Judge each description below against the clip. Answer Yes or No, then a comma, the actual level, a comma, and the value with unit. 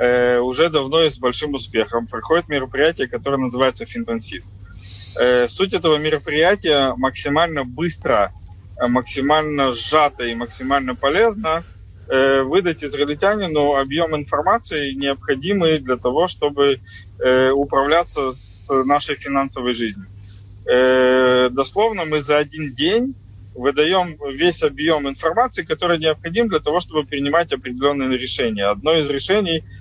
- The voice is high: No, medium, 140 Hz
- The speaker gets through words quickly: No, slow, 110 wpm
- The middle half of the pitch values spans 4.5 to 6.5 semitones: No, average, 4.1 semitones